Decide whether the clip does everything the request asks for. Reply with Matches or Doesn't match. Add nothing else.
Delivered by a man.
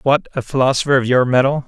Matches